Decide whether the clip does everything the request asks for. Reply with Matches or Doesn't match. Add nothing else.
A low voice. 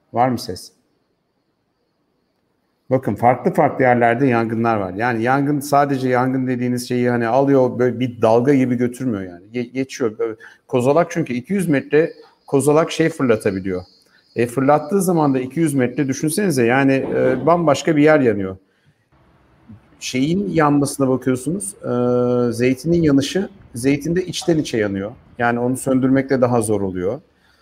Matches